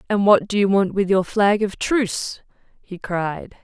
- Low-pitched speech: No, high, 195 Hz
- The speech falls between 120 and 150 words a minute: No, average, 200 wpm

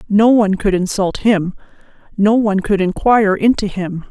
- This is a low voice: No, high, 200 Hz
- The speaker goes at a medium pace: Yes, average, 160 wpm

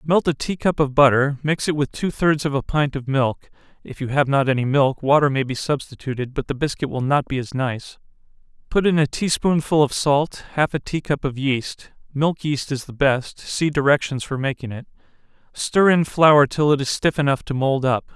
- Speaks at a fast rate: Yes, fast, 220 wpm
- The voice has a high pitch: No, medium, 140 Hz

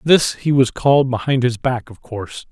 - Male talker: Yes, male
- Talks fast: Yes, fast, 215 wpm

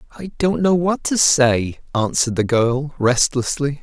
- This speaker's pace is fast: No, average, 155 wpm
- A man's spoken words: Yes, male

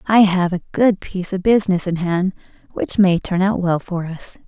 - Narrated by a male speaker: No, female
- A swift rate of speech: Yes, fast, 215 wpm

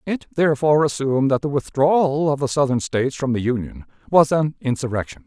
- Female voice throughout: No, male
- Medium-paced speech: Yes, average, 180 wpm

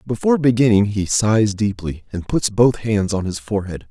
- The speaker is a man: Yes, male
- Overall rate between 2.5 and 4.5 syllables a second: No, 5.1 syllables/s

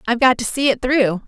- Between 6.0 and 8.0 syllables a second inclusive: Yes, 6.4 syllables/s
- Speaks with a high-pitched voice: Yes, high, 245 Hz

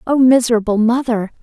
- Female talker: Yes, female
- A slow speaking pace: Yes, slow, 125 wpm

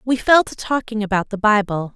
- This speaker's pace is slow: No, fast, 215 wpm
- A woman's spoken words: Yes, female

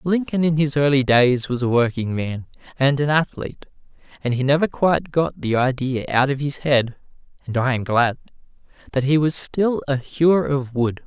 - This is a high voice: No, low, 135 Hz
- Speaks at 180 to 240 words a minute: Yes, average, 185 wpm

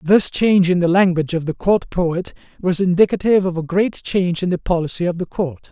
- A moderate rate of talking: No, fast, 220 wpm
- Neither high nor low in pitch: Yes, medium, 180 Hz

